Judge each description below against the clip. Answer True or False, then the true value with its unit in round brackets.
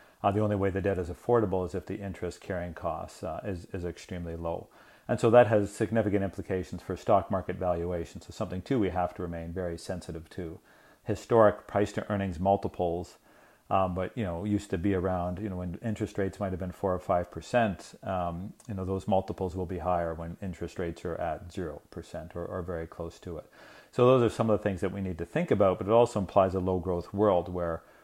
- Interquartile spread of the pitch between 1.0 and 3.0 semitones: True (2.5 semitones)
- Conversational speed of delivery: False (230 wpm)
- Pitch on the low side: True (95 Hz)